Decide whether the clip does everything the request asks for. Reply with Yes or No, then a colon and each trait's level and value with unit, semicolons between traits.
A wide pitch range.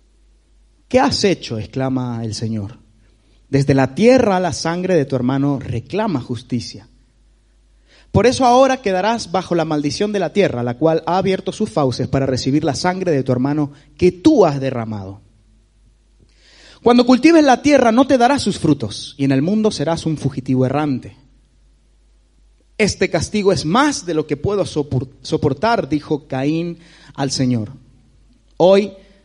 Yes: wide, 7.2 semitones